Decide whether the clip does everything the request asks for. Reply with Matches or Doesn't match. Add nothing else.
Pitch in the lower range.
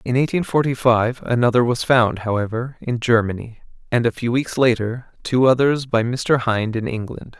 Matches